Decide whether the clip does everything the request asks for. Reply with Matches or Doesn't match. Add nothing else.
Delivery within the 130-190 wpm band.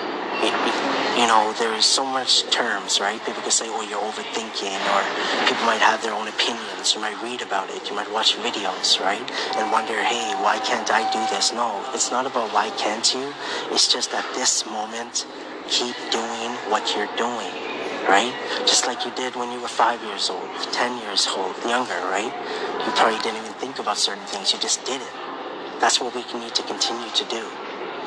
Doesn't match